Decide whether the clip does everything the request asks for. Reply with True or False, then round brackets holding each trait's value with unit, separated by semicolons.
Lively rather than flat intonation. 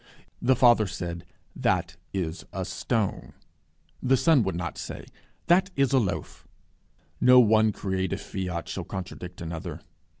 True (5.9 semitones)